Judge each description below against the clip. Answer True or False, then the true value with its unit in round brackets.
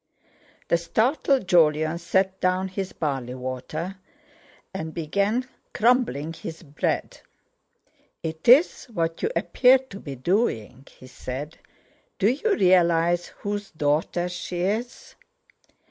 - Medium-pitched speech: True (175 Hz)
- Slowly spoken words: True (110 wpm)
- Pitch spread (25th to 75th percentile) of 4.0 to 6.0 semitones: True (4.7 semitones)